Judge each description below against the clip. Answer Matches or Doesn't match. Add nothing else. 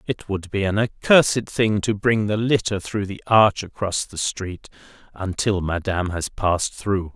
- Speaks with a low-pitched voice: Matches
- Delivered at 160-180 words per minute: Matches